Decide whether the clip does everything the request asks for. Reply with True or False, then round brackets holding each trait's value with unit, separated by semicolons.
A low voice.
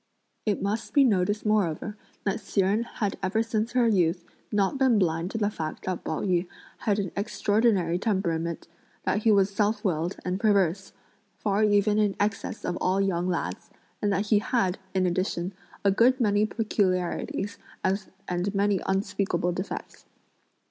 False (200 Hz)